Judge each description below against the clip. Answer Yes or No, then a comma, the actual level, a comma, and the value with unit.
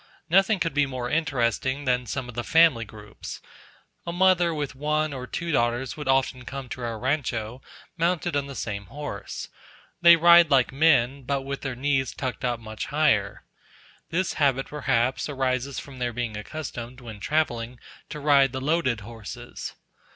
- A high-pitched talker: No, low, 135 Hz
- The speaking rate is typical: Yes, average, 165 wpm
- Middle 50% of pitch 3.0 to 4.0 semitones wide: Yes, average, 3.7 semitones